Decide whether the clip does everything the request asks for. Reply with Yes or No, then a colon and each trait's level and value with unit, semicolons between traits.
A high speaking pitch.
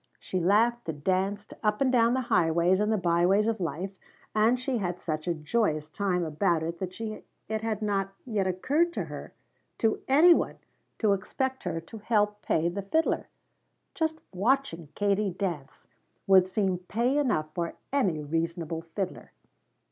Yes: high, 195 Hz